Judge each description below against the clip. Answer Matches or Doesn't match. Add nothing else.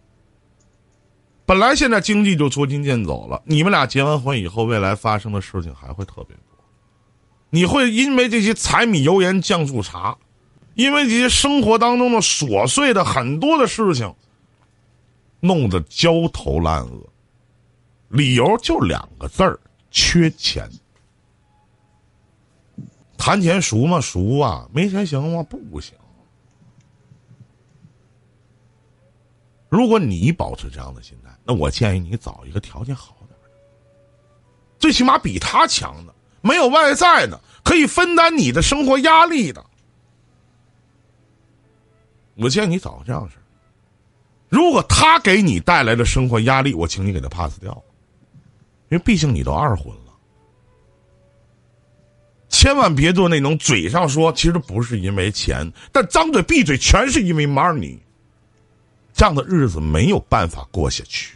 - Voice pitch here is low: Matches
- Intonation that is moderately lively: Doesn't match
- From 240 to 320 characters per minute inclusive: Doesn't match